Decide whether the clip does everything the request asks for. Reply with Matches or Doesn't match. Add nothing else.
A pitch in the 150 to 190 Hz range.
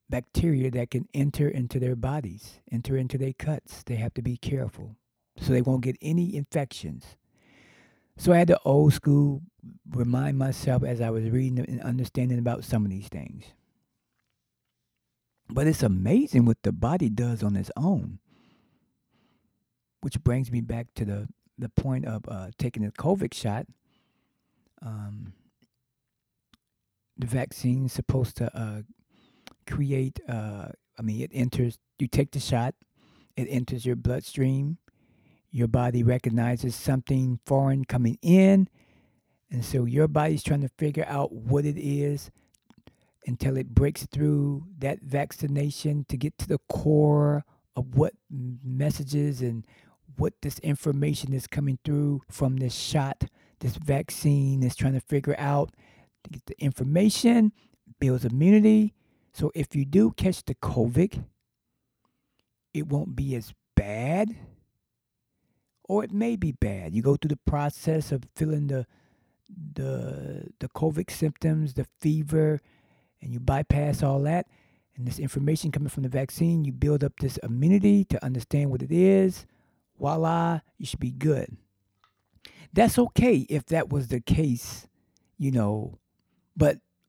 Doesn't match